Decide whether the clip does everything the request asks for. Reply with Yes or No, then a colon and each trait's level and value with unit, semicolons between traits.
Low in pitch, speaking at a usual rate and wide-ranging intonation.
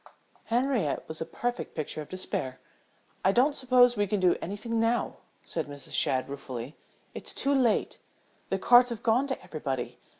No: high, 210 Hz; average, 165 wpm; wide, 8.1 semitones